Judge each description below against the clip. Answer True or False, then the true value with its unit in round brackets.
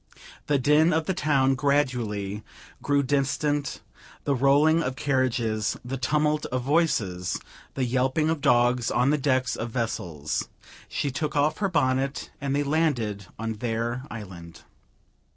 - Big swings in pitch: False (3.8 semitones)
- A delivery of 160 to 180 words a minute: False (140 wpm)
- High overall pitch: False (130 Hz)